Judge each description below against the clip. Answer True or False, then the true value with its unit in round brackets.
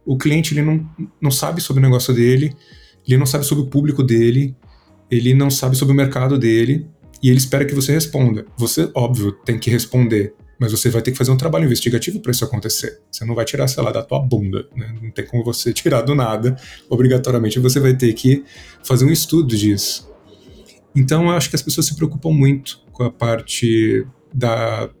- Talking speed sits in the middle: False (205 wpm)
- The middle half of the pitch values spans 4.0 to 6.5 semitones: False (3.5 semitones)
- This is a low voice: True (130 Hz)